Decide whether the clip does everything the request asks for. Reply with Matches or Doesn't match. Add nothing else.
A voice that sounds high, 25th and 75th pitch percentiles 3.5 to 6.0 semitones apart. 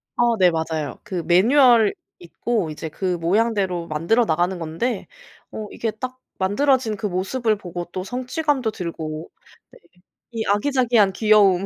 Matches